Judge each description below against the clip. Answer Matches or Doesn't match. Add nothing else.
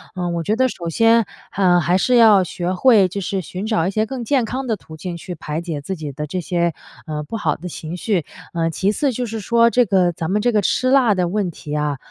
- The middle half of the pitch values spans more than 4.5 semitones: Matches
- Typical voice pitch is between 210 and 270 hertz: Doesn't match